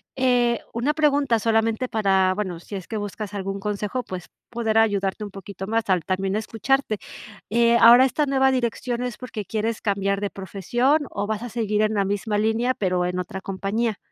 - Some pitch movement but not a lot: Yes, average, 3.2 semitones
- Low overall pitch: No, high, 215 Hz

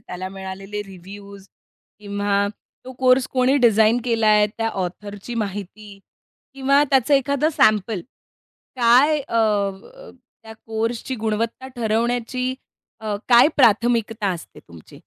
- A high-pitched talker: Yes, high, 220 Hz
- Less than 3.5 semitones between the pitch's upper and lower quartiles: No, average, 3.8 semitones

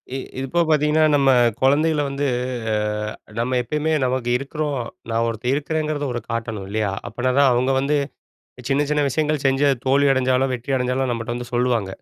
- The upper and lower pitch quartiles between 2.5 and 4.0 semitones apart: Yes, average, 3.2 semitones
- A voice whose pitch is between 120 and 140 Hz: Yes, low, 135 Hz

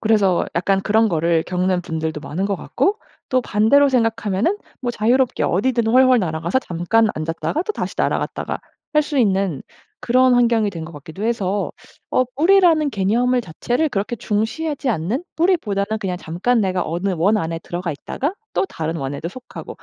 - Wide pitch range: Yes, wide, 6.1 semitones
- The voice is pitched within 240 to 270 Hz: No, high, 210 Hz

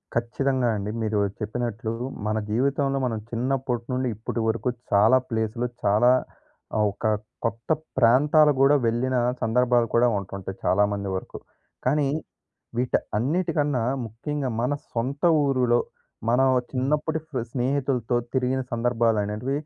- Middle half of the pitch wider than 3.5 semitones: No, average, 3.1 semitones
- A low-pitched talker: Yes, low, 125 Hz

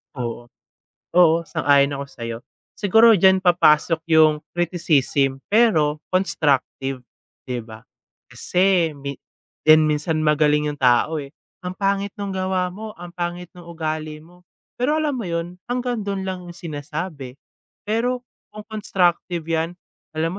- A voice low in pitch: No, medium, 170 Hz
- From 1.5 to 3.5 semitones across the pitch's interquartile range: No, average, 4.1 semitones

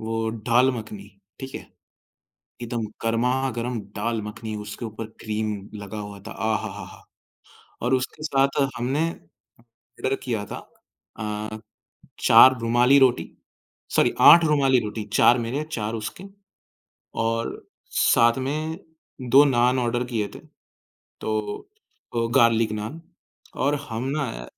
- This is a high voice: No, low, 115 Hz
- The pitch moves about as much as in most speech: Yes, average, 3.1 semitones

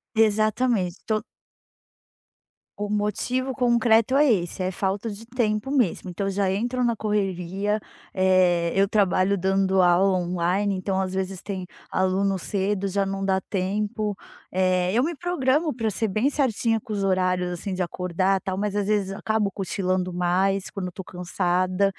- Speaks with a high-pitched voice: Yes, high, 195 Hz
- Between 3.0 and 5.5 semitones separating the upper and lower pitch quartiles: No, narrow, 2.6 semitones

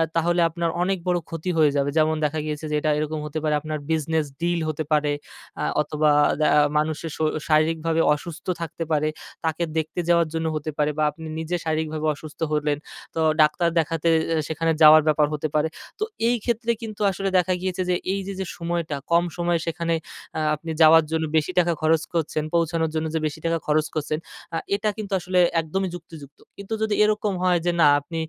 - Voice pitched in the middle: Yes, medium, 160 Hz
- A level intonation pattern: Yes, narrow, 2.0 semitones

